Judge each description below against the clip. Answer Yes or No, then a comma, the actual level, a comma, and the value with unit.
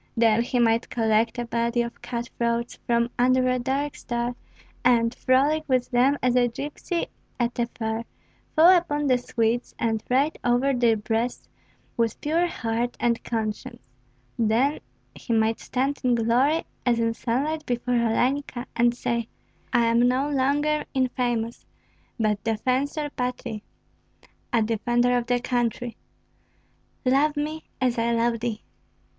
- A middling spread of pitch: No, narrow, 2.0 semitones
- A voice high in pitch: Yes, high, 240 Hz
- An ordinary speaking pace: Yes, average, 145 wpm